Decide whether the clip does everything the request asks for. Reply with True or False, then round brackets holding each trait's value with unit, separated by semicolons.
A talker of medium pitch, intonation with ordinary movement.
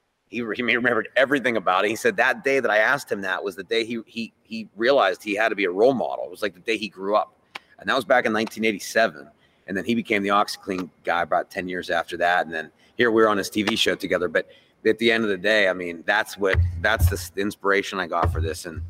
False (100 Hz; 3.4 semitones)